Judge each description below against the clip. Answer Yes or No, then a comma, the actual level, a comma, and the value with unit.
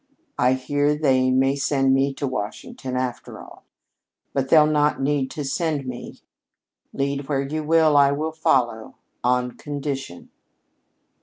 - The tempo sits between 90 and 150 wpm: Yes, average, 140 wpm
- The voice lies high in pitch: No, medium, 140 Hz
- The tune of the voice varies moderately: No, narrow, 2.3 semitones